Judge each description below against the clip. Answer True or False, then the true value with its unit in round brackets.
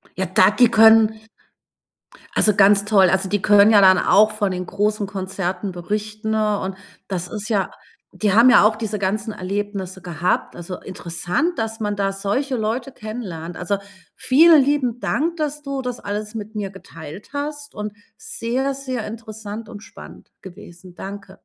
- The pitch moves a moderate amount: True (3.0 semitones)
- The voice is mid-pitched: False (210 Hz)